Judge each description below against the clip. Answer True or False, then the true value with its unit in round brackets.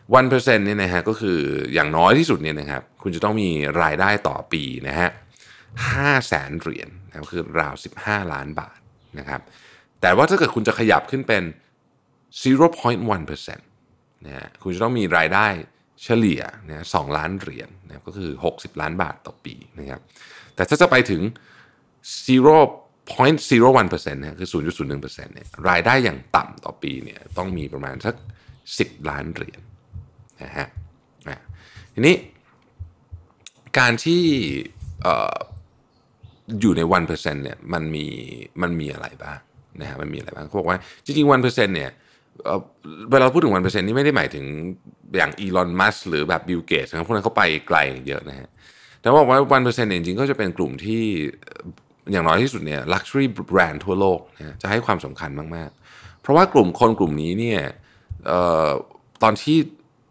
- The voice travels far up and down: True (6.9 semitones)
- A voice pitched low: True (100 Hz)